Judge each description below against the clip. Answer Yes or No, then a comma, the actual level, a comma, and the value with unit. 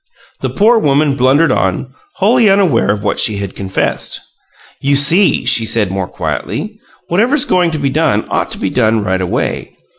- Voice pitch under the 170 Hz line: Yes, medium, 140 Hz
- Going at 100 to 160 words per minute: No, average, 175 wpm